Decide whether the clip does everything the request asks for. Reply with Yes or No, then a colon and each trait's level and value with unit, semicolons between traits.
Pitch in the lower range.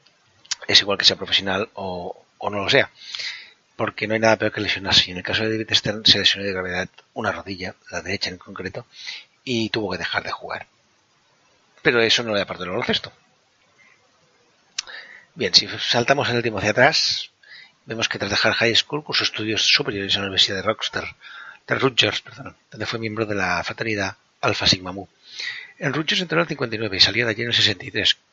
Yes: low, 110 Hz